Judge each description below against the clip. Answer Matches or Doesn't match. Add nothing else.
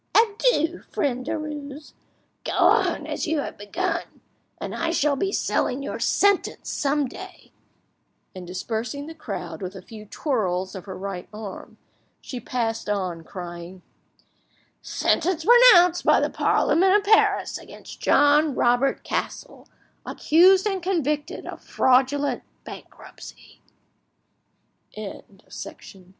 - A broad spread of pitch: Matches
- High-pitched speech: Matches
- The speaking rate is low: Matches